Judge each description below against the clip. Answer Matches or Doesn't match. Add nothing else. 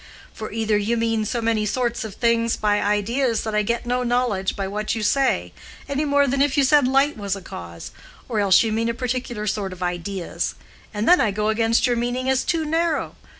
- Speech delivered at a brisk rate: Matches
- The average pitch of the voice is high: Matches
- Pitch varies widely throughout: Doesn't match